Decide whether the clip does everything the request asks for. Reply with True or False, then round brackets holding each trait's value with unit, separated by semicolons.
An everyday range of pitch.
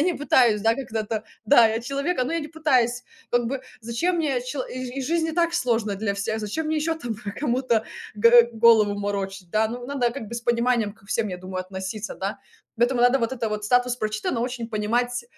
True (3.3 semitones)